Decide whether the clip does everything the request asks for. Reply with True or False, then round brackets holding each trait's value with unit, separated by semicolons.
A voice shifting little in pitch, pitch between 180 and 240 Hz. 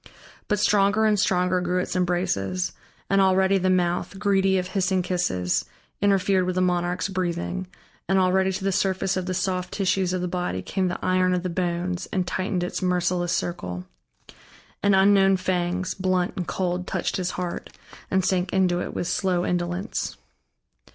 True (1.2 semitones; 185 Hz)